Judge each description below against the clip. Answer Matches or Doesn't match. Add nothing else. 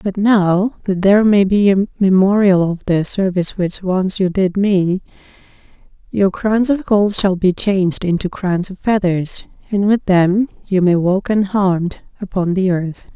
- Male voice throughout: Doesn't match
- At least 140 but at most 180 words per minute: Matches